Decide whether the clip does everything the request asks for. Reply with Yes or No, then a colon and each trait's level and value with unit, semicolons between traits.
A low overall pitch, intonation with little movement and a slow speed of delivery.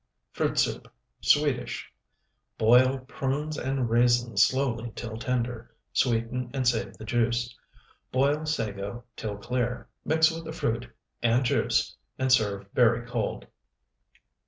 Yes: low, 120 Hz; narrow, 2.3 semitones; slow, 120 wpm